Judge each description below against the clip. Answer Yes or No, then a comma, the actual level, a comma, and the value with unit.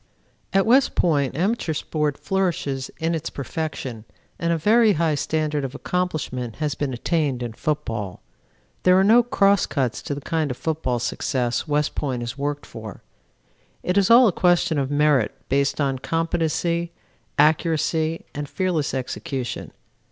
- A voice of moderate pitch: Yes, medium, 150 Hz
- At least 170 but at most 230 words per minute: No, average, 150 wpm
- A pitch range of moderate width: Yes, average, 3.9 semitones